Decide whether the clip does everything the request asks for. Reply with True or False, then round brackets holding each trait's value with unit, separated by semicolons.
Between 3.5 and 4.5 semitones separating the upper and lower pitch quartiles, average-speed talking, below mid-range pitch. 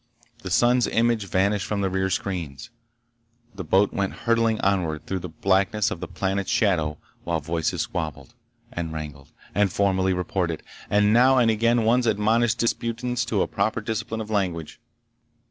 True (4.0 semitones; 160 wpm; 100 Hz)